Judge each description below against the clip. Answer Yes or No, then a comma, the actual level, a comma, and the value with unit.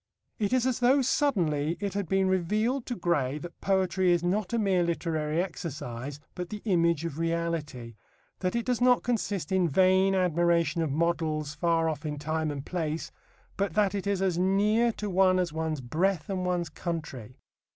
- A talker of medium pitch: Yes, medium, 175 Hz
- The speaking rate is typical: Yes, average, 180 wpm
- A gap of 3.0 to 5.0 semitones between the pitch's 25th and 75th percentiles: Yes, average, 3.6 semitones